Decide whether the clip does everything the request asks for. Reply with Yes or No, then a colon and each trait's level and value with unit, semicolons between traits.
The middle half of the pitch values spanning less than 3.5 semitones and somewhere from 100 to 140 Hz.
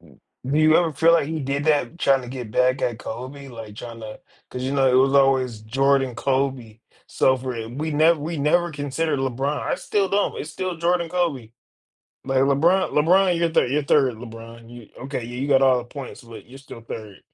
No: average, 4.0 semitones; low, 135 Hz